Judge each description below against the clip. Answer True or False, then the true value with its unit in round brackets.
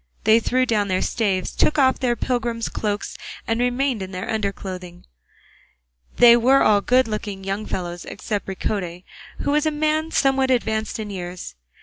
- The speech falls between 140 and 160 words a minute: False (170 wpm)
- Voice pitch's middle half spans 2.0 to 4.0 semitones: False (4.7 semitones)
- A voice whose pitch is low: False (220 Hz)